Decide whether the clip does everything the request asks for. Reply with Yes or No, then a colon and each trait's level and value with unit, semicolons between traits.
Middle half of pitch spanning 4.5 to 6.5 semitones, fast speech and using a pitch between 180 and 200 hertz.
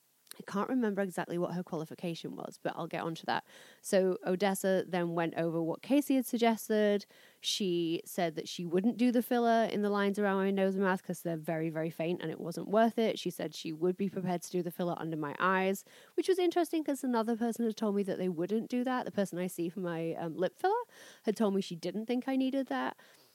Yes: average, 4.8 semitones; fast, 240 wpm; high, 190 Hz